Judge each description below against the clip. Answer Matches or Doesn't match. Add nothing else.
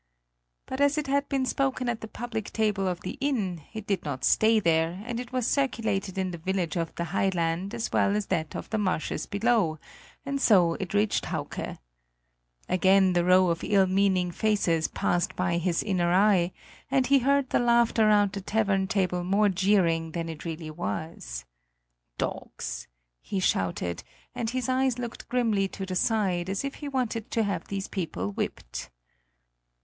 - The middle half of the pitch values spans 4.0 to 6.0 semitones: Matches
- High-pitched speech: Matches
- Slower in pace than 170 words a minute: Doesn't match